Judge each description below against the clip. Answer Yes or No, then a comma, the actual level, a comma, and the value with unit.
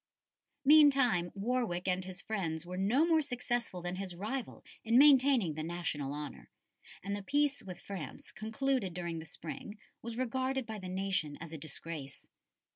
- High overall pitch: Yes, high, 195 Hz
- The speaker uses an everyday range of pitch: No, wide, 6.6 semitones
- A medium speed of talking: Yes, average, 160 wpm